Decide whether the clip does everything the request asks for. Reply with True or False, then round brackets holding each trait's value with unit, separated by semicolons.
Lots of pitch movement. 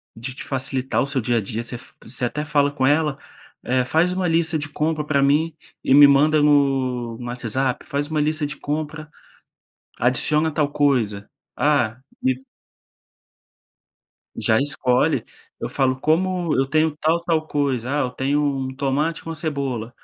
False (3.0 semitones)